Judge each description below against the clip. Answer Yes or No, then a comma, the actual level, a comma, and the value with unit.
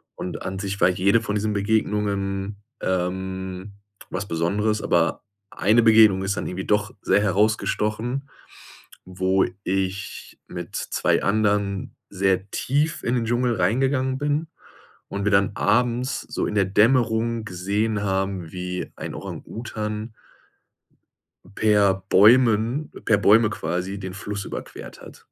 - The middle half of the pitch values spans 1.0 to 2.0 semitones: No, average, 2.7 semitones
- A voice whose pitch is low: Yes, low, 105 Hz